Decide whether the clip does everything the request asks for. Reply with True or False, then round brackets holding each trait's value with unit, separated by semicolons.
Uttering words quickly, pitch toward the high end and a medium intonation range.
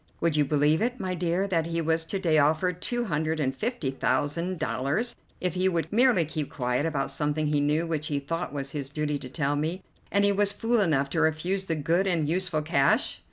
False (220 wpm; 160 Hz; 3.8 semitones)